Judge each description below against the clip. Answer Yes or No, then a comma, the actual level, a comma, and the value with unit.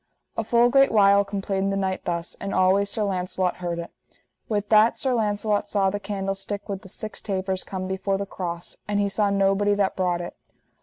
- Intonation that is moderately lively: No, narrow, 1.5 semitones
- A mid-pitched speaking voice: No, high, 195 Hz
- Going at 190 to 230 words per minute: Yes, average, 200 wpm